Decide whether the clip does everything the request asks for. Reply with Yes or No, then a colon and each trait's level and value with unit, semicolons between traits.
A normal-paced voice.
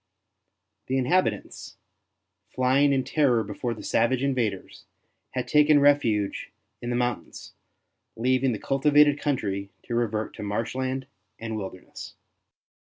No: slow, 120 wpm